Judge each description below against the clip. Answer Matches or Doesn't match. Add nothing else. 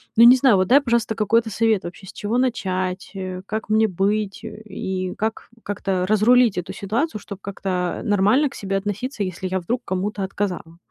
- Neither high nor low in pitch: Doesn't match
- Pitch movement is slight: Doesn't match